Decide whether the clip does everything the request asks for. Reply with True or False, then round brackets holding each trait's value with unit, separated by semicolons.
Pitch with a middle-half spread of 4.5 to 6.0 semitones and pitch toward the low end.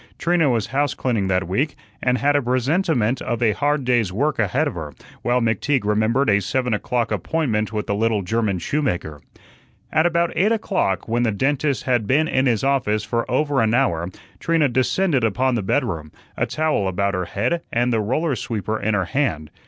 True (5.3 semitones; 120 Hz)